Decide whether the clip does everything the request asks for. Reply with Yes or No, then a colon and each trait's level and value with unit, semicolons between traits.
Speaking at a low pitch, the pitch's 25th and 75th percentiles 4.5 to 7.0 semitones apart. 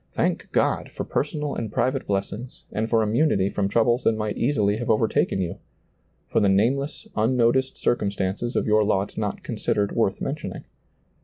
No: low, 110 Hz; average, 3.8 semitones